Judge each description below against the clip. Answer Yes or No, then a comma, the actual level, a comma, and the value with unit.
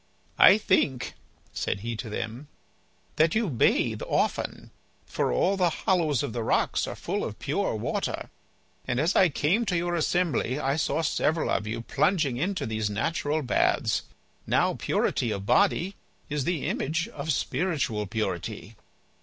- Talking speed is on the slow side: No, average, 155 wpm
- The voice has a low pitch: No, medium, 150 Hz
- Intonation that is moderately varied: No, wide, 6.8 semitones